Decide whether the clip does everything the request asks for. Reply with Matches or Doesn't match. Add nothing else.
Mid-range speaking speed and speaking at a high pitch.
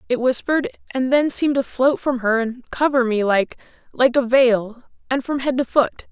Matches